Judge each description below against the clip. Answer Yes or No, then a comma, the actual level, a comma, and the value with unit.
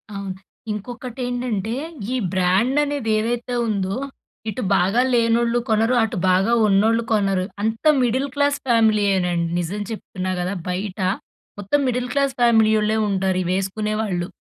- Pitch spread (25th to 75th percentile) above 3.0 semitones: Yes, average, 3.9 semitones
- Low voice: No, high, 215 Hz